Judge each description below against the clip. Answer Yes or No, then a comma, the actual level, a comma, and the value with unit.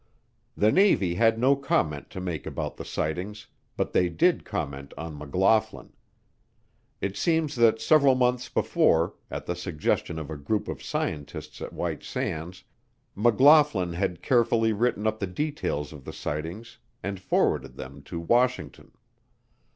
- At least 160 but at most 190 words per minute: No, average, 145 wpm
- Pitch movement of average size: No, wide, 6.4 semitones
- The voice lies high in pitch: No, low, 100 Hz